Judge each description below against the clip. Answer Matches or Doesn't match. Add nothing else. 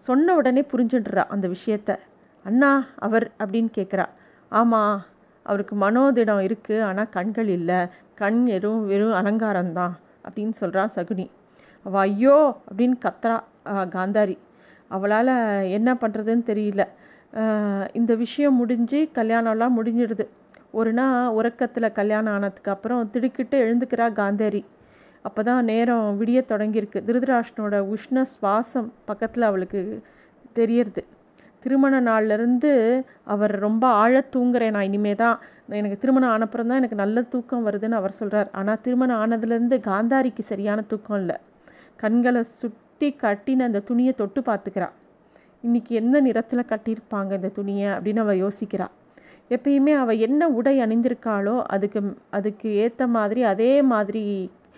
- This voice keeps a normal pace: Matches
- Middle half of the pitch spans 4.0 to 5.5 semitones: Doesn't match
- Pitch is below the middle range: Doesn't match